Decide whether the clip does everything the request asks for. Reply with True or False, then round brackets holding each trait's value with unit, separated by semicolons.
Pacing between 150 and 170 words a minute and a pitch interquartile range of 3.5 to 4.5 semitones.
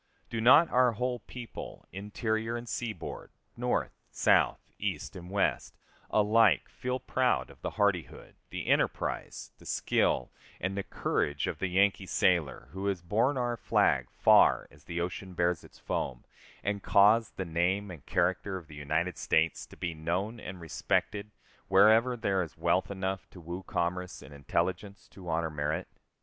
True (160 wpm; 4.0 semitones)